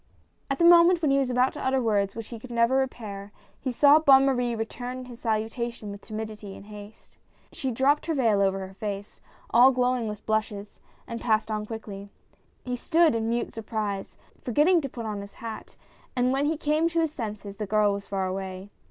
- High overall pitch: Yes, high, 230 Hz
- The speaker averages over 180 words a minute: Yes, fast, 205 wpm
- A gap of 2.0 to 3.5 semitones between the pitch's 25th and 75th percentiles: No, average, 4.1 semitones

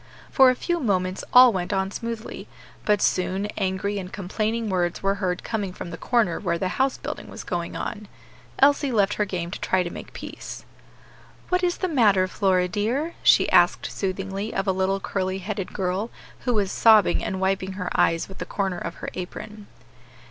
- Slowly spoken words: No, average, 190 wpm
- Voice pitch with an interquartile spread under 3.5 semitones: Yes, average, 2.8 semitones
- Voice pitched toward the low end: No, high, 195 Hz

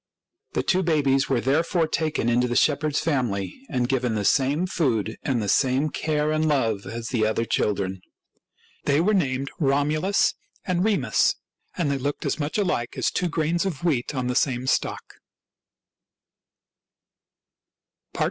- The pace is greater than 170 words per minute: No, average, 150 wpm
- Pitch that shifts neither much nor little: Yes, average, 4.4 semitones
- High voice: No, medium, 140 Hz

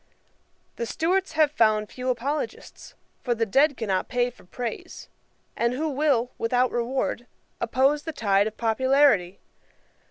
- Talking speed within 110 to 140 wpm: Yes, slow, 135 wpm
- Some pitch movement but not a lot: Yes, average, 3.9 semitones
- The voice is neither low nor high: No, high, 245 Hz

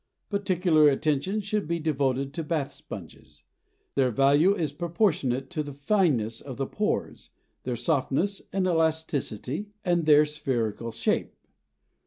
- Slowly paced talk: Yes, slow, 130 wpm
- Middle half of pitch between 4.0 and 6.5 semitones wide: Yes, average, 4.6 semitones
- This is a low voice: No, medium, 150 Hz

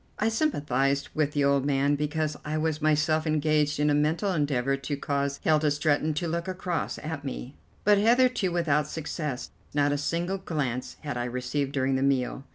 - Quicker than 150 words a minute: Yes, average, 180 wpm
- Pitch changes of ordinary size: No, narrow, 2.3 semitones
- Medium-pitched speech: Yes, medium, 150 Hz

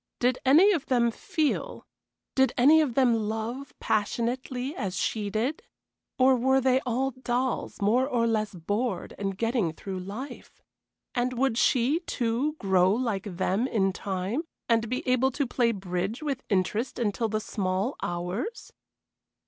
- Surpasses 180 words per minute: No, average, 150 wpm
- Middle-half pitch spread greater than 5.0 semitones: No, average, 4.3 semitones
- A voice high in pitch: Yes, high, 235 Hz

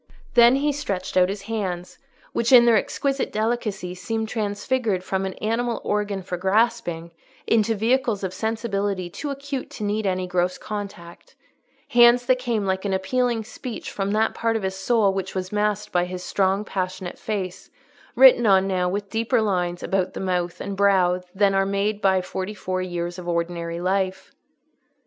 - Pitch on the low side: No, high, 200 Hz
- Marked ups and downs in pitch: No, average, 3.3 semitones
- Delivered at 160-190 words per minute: Yes, average, 170 wpm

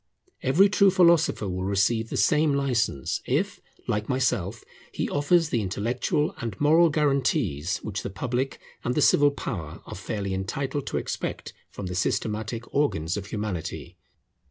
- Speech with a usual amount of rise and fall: No, wide, 6.7 semitones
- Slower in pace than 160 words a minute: Yes, average, 150 wpm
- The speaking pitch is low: Yes, low, 115 Hz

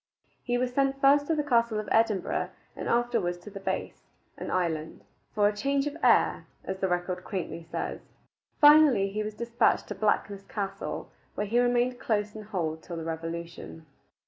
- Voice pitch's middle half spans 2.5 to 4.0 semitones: No, average, 5.1 semitones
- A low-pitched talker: No, high, 210 Hz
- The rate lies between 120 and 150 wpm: No, average, 175 wpm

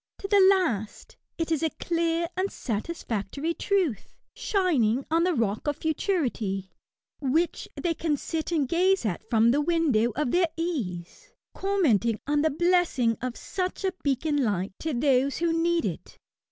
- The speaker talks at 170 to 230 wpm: No, average, 155 wpm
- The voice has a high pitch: Yes, very high, 310 Hz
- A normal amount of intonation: No, wide, 6.4 semitones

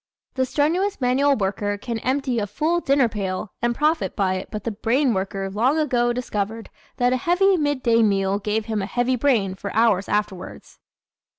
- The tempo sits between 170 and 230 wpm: Yes, average, 180 wpm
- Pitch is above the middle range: Yes, high, 230 Hz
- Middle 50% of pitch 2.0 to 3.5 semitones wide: No, average, 4.9 semitones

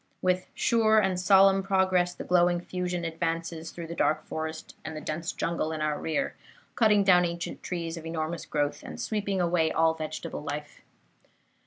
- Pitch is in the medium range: Yes, medium, 170 Hz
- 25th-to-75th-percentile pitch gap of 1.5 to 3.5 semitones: Yes, narrow, 2.5 semitones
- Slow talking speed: No, average, 170 wpm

